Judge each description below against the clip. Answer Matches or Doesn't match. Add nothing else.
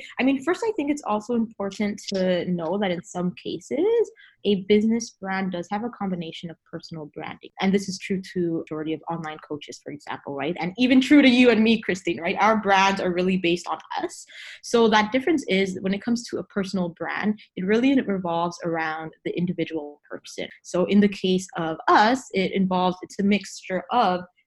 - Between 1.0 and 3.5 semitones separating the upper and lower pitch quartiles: Doesn't match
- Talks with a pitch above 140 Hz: Matches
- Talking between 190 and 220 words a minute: Matches